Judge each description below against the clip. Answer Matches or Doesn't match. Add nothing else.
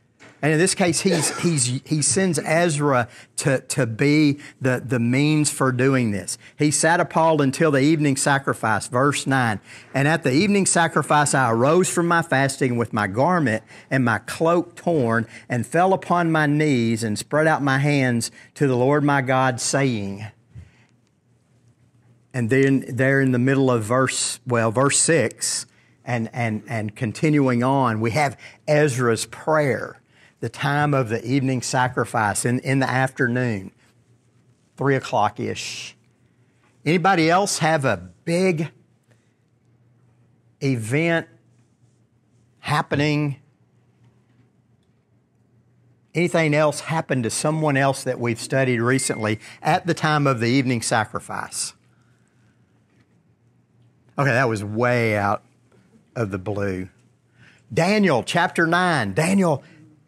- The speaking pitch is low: Matches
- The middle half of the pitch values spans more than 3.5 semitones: Matches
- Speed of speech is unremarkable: Doesn't match